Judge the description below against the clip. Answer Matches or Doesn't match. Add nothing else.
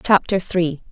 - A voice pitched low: Doesn't match